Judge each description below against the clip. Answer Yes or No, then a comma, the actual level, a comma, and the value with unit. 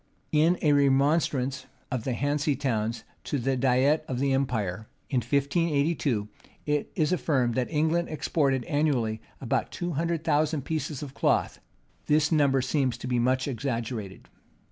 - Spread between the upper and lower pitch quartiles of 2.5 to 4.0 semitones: Yes, average, 3.3 semitones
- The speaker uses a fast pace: No, average, 145 wpm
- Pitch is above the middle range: No, medium, 140 Hz